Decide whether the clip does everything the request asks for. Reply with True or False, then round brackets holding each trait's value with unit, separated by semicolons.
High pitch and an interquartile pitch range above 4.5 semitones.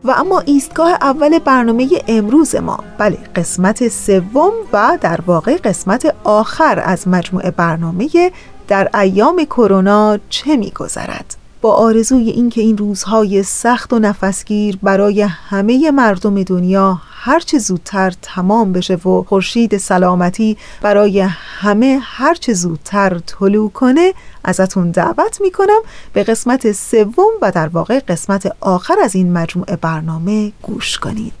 True (210 Hz; 5.1 semitones)